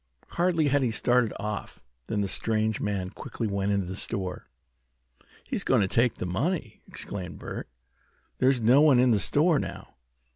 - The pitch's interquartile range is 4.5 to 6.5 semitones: Yes, average, 4.9 semitones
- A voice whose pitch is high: No, low, 110 Hz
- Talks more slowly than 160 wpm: No, average, 170 wpm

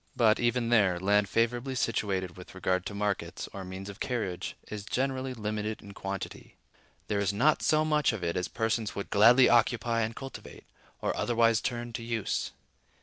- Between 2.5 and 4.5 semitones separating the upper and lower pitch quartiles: Yes, average, 3.2 semitones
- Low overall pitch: Yes, low, 110 Hz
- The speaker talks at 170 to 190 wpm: Yes, average, 175 wpm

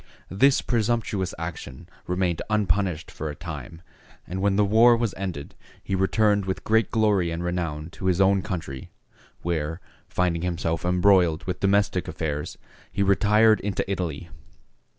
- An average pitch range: Yes, average, 3.4 semitones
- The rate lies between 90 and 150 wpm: Yes, average, 145 wpm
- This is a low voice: Yes, very low, 95 Hz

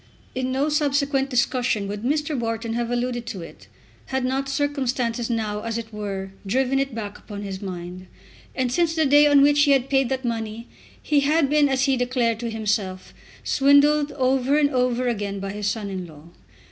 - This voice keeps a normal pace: Yes, average, 190 wpm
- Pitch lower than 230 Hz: No, very high, 250 Hz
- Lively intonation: No, average, 4.5 semitones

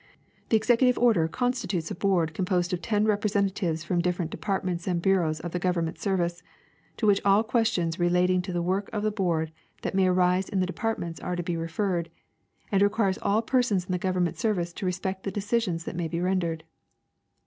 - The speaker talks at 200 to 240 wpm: Yes, fast, 205 wpm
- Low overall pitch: No, medium, 185 Hz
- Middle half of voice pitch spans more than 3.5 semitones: No, average, 2.8 semitones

